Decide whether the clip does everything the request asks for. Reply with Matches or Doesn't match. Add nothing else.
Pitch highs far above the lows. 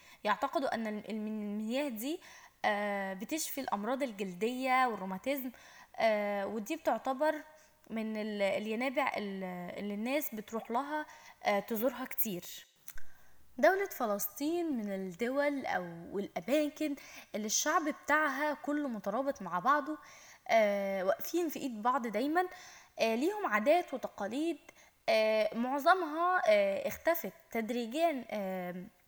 Matches